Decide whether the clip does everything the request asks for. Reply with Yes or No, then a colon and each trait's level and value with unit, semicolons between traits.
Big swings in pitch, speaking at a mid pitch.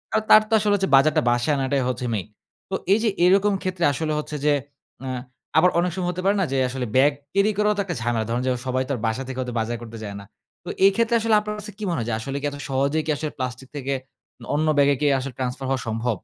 Yes: wide, 6.7 semitones; medium, 145 Hz